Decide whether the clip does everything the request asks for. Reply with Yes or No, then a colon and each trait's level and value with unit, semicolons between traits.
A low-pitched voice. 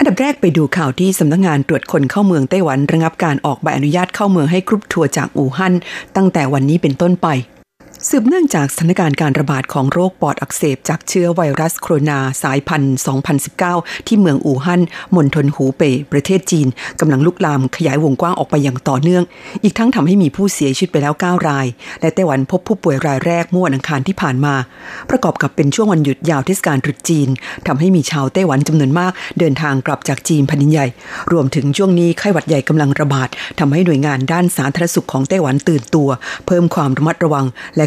No: medium, 155 Hz